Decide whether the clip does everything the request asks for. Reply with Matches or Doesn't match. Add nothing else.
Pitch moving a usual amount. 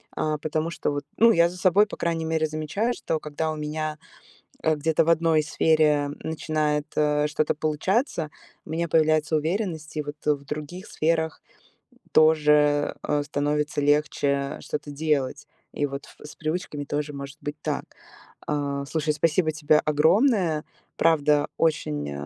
Doesn't match